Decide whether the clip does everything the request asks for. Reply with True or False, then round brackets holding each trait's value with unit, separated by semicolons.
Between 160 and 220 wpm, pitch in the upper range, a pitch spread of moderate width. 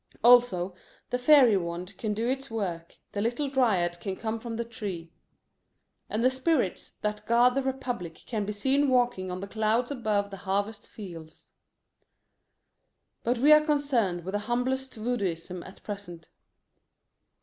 False (150 wpm; 220 Hz; 4.6 semitones)